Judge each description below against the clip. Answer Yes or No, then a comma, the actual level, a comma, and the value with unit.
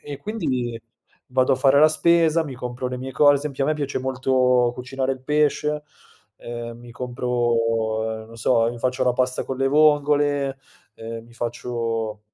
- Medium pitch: No, low, 130 Hz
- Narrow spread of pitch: No, average, 3.2 semitones